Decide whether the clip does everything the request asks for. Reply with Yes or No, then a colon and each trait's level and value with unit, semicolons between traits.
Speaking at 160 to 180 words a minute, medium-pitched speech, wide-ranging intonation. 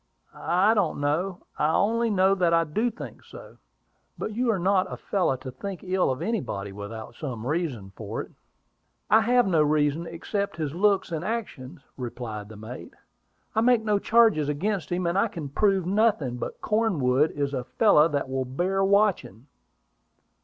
Yes: average, 175 wpm; medium, 170 Hz; wide, 7.1 semitones